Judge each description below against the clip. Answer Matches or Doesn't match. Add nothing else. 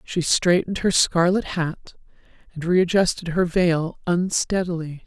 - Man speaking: Doesn't match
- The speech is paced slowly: Matches